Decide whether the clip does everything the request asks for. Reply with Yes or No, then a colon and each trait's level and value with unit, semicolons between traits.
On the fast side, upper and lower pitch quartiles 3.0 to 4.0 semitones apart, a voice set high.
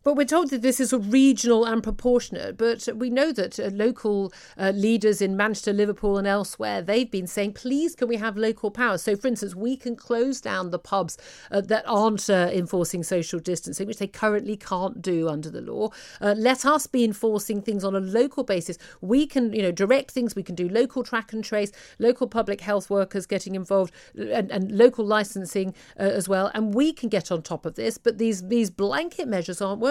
Yes: fast, 215 wpm; average, 3.6 semitones; high, 215 Hz